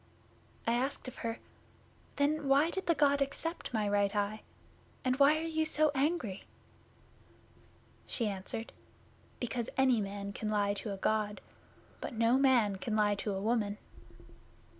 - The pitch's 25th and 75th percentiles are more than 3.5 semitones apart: Yes, average, 5.2 semitones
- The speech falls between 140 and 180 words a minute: Yes, average, 150 wpm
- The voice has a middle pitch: No, high, 230 Hz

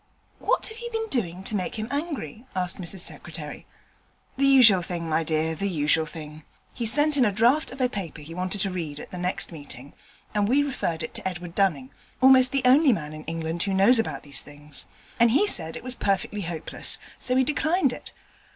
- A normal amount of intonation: No, wide, 7.8 semitones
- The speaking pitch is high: Yes, high, 195 Hz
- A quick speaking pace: Yes, fast, 210 wpm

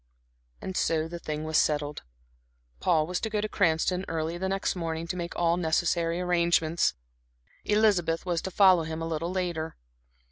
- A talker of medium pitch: Yes, medium, 170 Hz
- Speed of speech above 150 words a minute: Yes, average, 170 wpm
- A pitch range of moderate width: No, narrow, 2.1 semitones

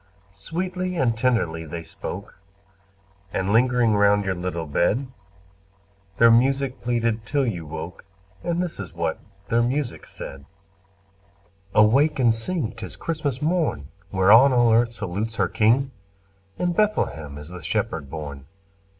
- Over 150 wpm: No, slow, 135 wpm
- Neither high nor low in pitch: No, low, 115 Hz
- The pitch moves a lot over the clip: Yes, wide, 7.3 semitones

